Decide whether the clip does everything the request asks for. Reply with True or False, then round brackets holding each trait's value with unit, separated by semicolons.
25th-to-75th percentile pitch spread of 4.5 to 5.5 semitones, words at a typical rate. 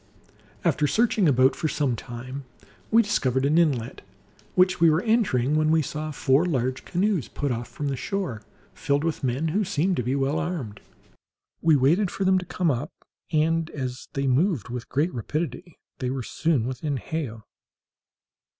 True (4.8 semitones; 170 wpm)